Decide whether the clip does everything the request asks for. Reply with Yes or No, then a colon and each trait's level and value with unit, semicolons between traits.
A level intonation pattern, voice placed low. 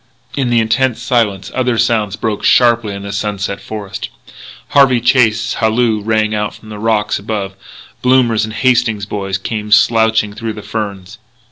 Yes: narrow, 2.2 semitones; low, 110 Hz